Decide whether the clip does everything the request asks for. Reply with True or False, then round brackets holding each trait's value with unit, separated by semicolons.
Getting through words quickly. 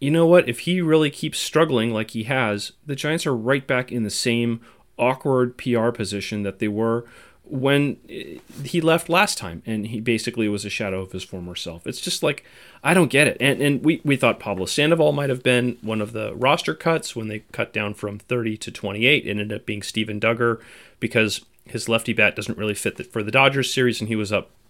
True (225 wpm)